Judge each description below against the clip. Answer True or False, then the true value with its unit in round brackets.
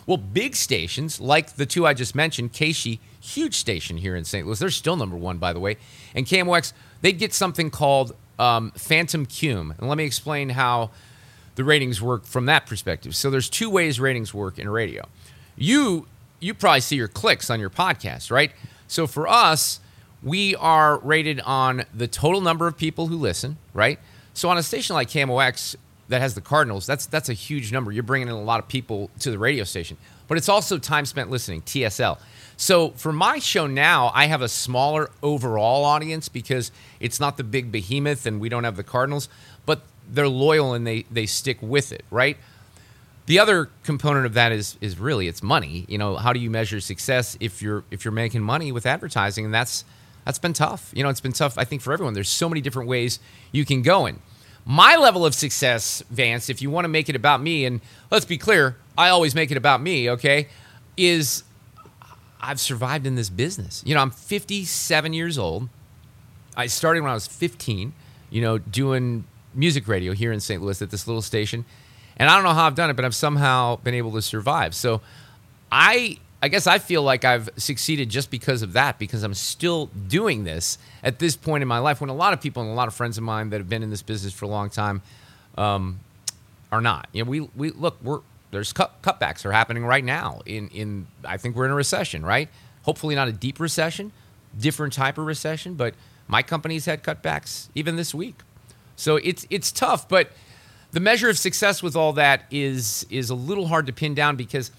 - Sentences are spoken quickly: True (210 wpm)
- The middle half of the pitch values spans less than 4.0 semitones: False (5.2 semitones)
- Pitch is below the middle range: True (130 Hz)